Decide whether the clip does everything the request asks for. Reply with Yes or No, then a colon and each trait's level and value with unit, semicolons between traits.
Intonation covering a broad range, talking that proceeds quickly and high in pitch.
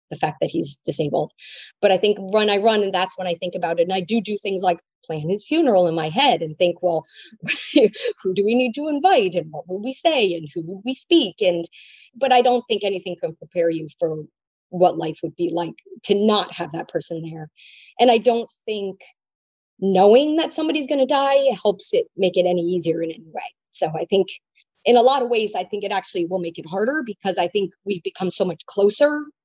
Yes: wide, 5.7 semitones; fast, 230 wpm; high, 195 Hz